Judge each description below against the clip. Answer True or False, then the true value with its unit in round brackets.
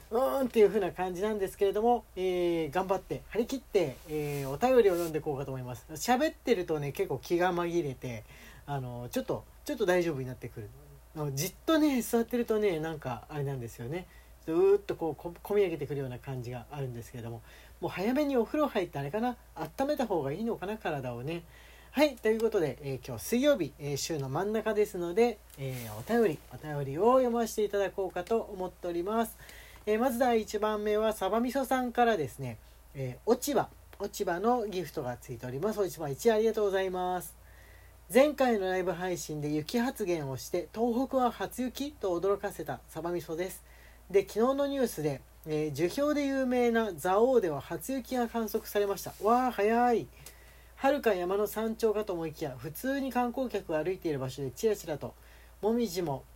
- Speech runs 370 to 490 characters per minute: True (390 characters per minute)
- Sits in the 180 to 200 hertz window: True (190 Hz)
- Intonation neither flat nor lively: False (7.7 semitones)